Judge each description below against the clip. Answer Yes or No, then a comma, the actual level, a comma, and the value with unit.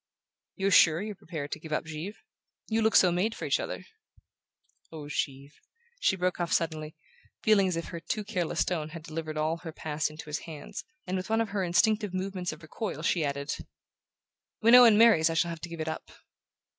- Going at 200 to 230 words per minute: Yes, fast, 205 wpm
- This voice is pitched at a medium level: Yes, medium, 170 Hz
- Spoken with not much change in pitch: No, average, 4.0 semitones